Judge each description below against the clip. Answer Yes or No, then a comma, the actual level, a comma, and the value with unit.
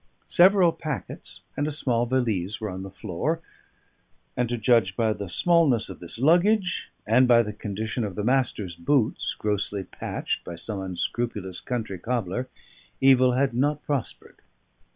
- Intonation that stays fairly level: No, average, 5.0 semitones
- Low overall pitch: Yes, low, 115 Hz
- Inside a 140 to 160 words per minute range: Yes, average, 150 wpm